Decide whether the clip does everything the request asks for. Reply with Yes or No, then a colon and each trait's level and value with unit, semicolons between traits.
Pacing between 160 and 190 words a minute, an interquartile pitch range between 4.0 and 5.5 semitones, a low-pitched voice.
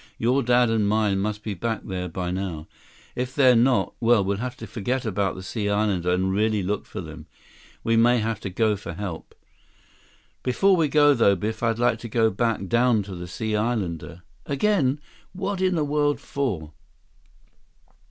Yes: average, 180 wpm; average, 4.3 semitones; low, 110 Hz